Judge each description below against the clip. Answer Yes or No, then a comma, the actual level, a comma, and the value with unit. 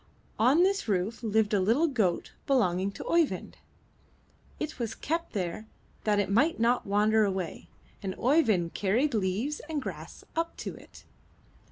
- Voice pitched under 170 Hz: No, high, 220 Hz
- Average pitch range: No, wide, 6.4 semitones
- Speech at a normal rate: Yes, average, 150 wpm